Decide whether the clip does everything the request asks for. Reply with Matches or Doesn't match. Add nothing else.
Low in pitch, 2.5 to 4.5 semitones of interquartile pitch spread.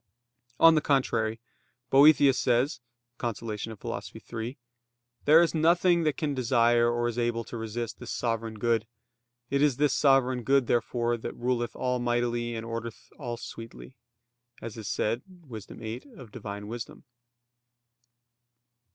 Matches